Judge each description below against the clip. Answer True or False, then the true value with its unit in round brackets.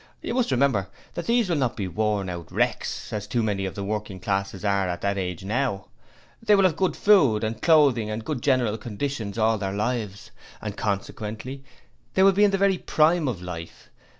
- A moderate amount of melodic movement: False (6.3 semitones)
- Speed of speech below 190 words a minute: False (205 wpm)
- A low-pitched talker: True (110 Hz)